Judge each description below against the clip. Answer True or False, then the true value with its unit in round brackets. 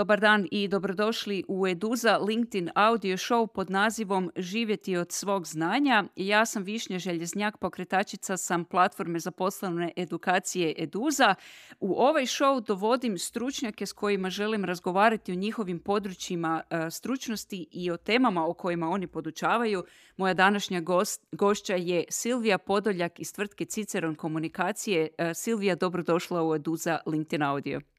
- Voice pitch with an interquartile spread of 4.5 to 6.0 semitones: False (3.5 semitones)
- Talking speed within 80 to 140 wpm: True (135 wpm)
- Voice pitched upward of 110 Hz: True (190 Hz)